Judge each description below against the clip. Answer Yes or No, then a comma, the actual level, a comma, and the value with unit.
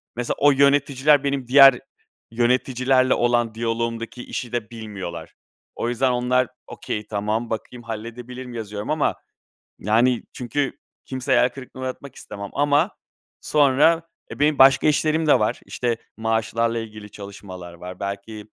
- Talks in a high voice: No, low, 120 Hz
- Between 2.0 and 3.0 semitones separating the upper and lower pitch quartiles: No, average, 3.4 semitones